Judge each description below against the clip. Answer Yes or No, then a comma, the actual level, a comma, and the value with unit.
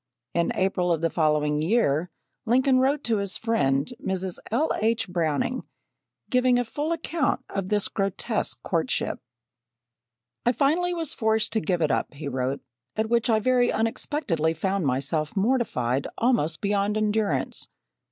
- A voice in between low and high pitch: No, high, 205 Hz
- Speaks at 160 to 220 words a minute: No, average, 145 wpm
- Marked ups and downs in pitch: Yes, wide, 7.1 semitones